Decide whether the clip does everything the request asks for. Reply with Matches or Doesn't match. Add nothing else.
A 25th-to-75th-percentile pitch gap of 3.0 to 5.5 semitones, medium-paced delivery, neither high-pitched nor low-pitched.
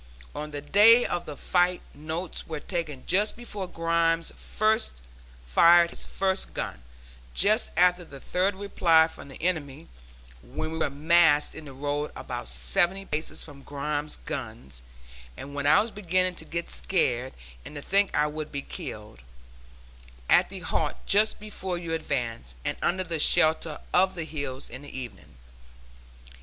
Matches